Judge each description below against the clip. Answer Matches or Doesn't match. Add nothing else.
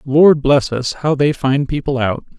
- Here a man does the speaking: Matches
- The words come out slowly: Doesn't match